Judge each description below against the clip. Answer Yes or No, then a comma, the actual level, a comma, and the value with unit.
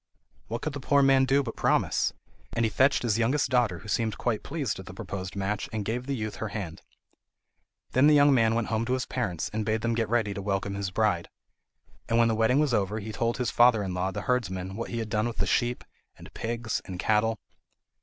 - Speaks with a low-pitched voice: Yes, low, 115 Hz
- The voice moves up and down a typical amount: Yes, average, 3.4 semitones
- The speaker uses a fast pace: Yes, fast, 235 wpm